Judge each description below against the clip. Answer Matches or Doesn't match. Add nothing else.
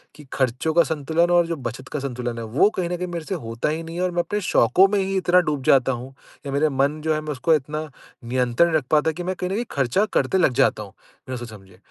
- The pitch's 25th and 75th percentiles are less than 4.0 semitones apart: Doesn't match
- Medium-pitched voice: Matches